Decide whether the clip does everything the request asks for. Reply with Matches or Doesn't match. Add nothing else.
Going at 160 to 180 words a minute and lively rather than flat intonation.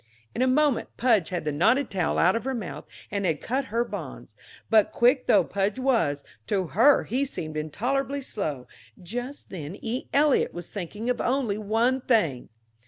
Matches